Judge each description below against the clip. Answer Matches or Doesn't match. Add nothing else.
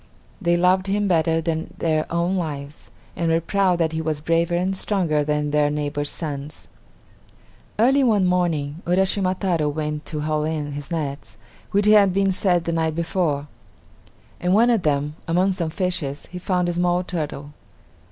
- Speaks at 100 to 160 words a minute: Doesn't match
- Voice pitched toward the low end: Doesn't match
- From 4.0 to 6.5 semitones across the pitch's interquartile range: Doesn't match